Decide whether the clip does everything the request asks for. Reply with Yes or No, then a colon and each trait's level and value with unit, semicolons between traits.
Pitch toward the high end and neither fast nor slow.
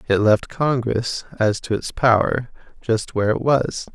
No: low, 115 Hz; average, 165 wpm